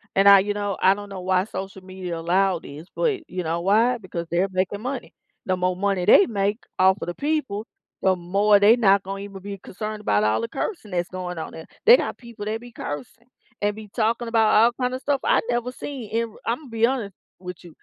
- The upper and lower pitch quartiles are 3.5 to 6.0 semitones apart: Yes, average, 3.8 semitones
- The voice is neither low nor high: No, high, 200 Hz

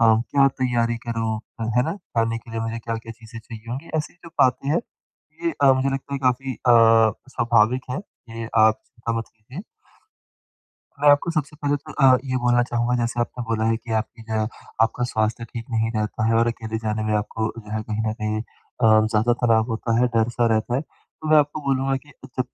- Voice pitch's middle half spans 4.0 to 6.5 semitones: No, average, 2.7 semitones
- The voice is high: No, low, 115 Hz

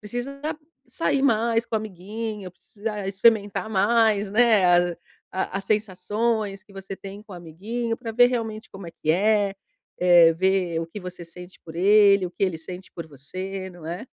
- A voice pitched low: No, high, 195 Hz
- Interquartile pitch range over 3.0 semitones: Yes, average, 3.4 semitones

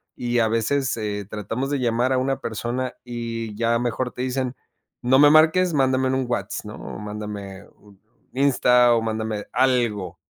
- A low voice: Yes, low, 120 Hz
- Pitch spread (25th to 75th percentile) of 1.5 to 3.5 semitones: Yes, average, 3.0 semitones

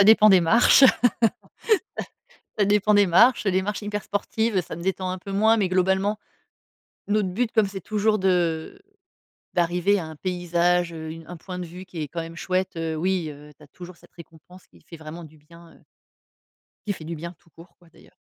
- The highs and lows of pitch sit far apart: No, average, 3.3 semitones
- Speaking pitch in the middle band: Yes, medium, 180 Hz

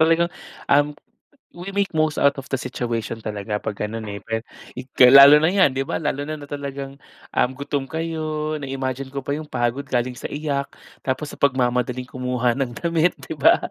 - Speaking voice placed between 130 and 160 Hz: Yes, medium, 140 Hz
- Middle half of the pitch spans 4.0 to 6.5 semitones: No, average, 3.3 semitones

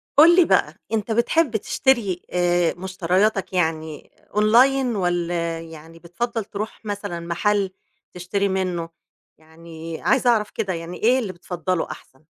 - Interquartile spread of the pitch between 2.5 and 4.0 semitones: No, average, 4.4 semitones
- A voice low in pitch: No, medium, 185 Hz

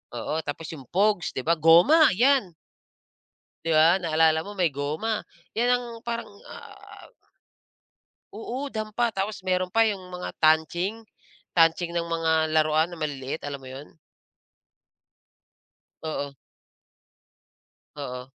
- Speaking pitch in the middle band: Yes, medium, 170 Hz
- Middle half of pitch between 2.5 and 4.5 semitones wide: No, average, 5.2 semitones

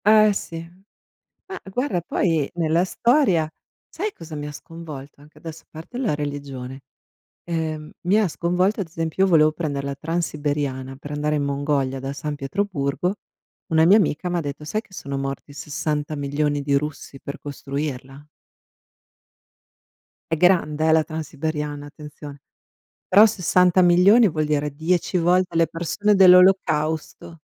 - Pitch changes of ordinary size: Yes, average, 3.7 semitones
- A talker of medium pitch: Yes, medium, 155 Hz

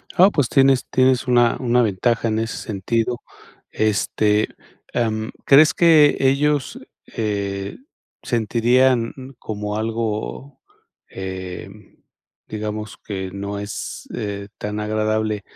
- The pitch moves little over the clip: No, average, 3.1 semitones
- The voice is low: Yes, low, 110 Hz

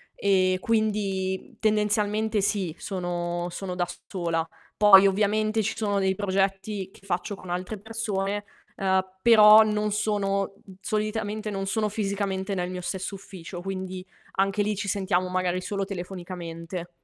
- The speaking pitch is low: No, high, 195 Hz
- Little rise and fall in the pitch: Yes, narrow, 2.2 semitones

